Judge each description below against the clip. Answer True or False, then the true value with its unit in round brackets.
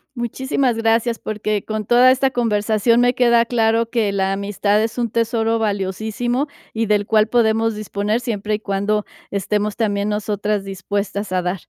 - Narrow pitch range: True (2.2 semitones)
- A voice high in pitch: True (215 Hz)